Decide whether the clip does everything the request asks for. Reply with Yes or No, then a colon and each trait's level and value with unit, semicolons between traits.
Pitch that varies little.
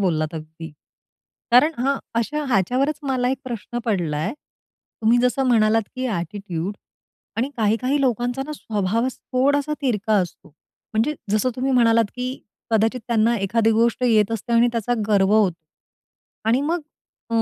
No: average, 3.6 semitones